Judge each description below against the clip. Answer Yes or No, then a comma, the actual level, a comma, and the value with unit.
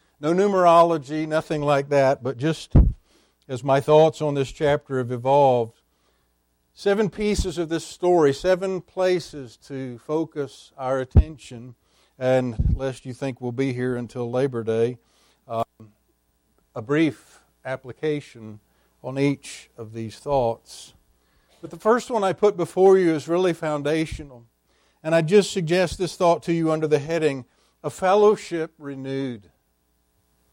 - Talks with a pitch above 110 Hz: Yes, medium, 140 Hz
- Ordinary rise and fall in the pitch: No, wide, 5.8 semitones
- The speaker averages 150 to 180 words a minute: No, average, 140 wpm